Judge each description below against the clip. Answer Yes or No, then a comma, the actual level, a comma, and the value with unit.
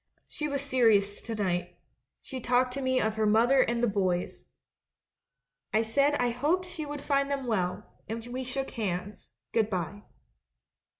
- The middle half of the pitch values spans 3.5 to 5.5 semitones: Yes, average, 4.6 semitones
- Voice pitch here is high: Yes, high, 240 Hz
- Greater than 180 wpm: No, average, 170 wpm